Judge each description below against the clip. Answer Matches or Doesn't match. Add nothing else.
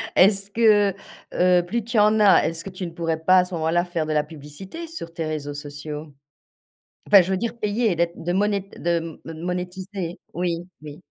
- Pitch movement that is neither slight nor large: Matches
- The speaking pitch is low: Doesn't match